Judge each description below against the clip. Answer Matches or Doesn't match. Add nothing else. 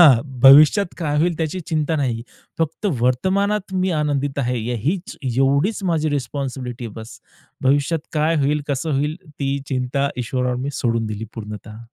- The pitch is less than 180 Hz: Matches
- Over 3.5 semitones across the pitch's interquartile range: Matches